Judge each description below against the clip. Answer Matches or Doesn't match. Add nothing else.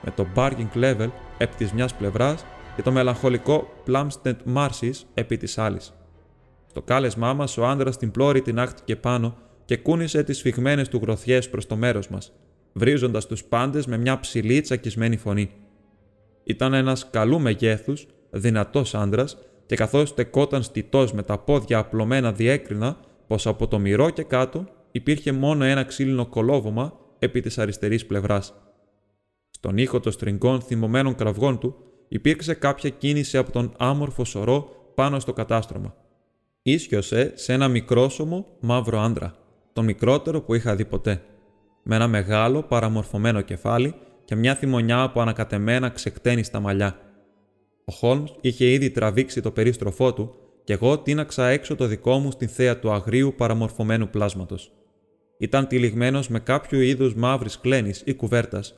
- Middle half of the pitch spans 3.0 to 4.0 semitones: Matches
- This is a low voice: Matches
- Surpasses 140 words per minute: Matches